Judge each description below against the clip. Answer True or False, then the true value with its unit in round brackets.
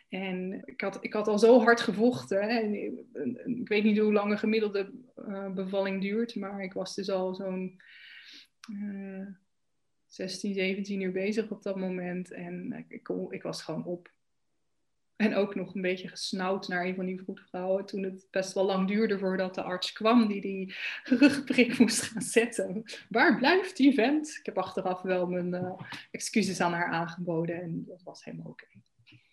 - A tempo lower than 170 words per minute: False (180 wpm)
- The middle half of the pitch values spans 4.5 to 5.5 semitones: False (3.1 semitones)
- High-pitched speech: True (195 Hz)